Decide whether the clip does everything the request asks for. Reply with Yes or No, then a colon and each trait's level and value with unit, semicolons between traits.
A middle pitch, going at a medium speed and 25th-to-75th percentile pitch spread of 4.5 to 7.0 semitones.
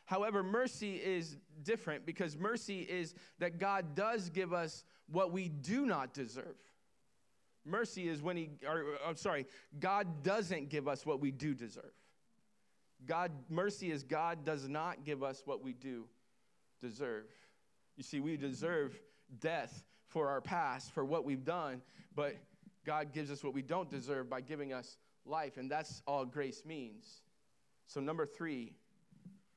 Yes: medium, 160 Hz; average, 155 wpm; average, 4.9 semitones